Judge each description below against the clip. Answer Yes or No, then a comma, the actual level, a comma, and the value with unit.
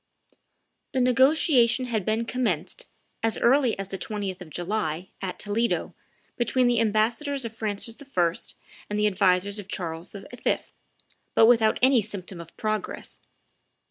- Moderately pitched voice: No, high, 215 Hz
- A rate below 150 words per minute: Yes, average, 140 wpm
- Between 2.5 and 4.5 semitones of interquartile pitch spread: Yes, average, 3.7 semitones